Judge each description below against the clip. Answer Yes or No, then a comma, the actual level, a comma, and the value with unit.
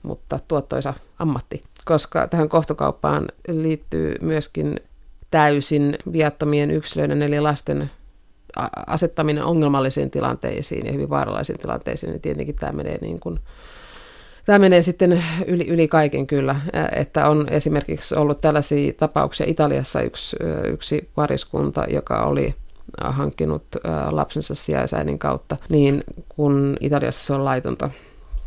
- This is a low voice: No, medium, 145 Hz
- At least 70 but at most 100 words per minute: No, average, 115 wpm